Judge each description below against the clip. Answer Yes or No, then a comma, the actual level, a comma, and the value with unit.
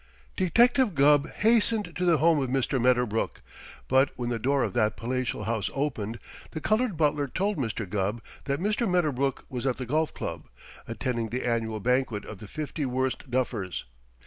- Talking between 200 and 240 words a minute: No, average, 170 wpm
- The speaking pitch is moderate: No, low, 130 Hz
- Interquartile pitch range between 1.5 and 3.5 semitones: No, average, 5.0 semitones